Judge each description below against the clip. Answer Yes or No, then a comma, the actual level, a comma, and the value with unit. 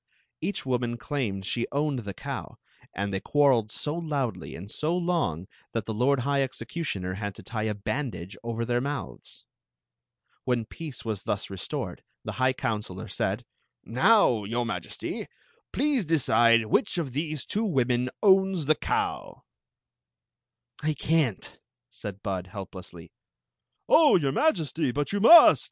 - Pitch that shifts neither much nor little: No, wide, 6.2 semitones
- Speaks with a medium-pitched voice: No, low, 125 Hz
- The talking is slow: No, average, 150 wpm